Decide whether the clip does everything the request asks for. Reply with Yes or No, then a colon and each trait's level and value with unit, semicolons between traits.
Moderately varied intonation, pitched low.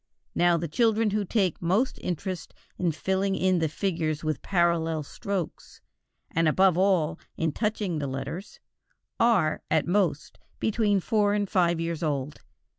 No: average, 3.9 semitones; medium, 175 Hz